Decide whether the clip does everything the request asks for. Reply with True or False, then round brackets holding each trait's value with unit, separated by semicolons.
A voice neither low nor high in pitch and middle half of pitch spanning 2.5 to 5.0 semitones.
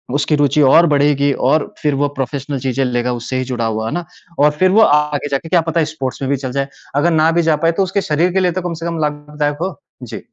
True (145 Hz; 3.3 semitones)